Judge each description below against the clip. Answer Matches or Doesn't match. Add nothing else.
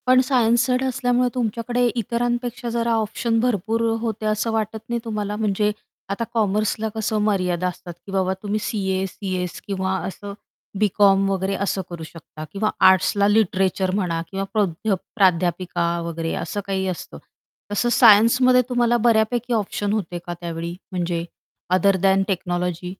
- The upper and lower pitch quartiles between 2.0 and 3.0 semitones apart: Doesn't match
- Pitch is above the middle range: Matches